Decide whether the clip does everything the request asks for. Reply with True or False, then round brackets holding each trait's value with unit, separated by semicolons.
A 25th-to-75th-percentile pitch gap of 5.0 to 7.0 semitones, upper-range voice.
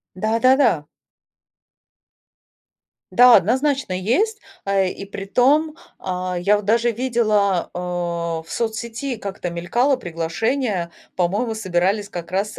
True (5.3 semitones; 205 Hz)